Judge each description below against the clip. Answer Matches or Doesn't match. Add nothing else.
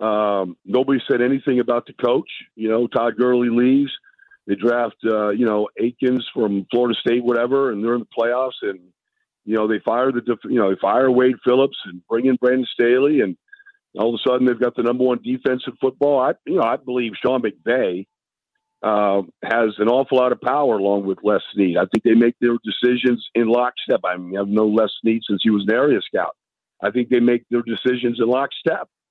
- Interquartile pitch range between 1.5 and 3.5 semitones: Matches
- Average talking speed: Doesn't match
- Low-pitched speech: Matches